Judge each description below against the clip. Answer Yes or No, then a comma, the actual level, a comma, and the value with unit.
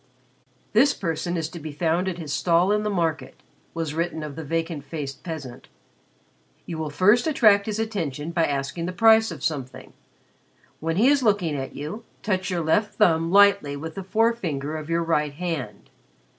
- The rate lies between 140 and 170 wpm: No, average, 180 wpm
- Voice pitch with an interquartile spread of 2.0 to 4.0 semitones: No, average, 4.8 semitones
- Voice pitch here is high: No, medium, 165 Hz